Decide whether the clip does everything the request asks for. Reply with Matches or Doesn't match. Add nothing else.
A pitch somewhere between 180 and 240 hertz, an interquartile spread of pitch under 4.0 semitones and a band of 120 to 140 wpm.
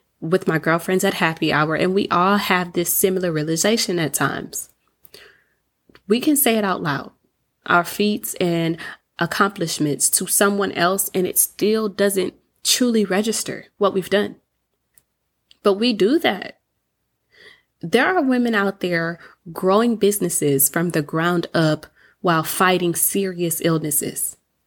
Matches